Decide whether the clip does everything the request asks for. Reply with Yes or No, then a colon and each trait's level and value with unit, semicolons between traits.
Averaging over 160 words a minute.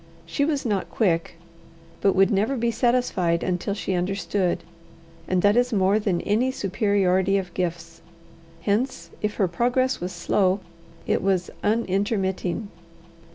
No: slow, 135 wpm